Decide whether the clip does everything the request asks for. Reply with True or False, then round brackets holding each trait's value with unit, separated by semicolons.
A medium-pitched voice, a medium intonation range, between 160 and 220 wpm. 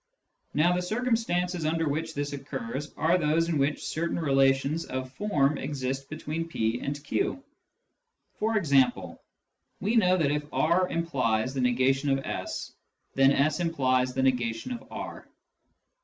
False (150 Hz; 3.9 semitones; 145 wpm)